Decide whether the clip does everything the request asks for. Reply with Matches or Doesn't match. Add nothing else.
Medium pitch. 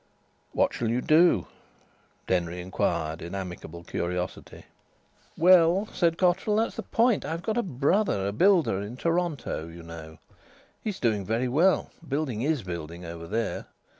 Doesn't match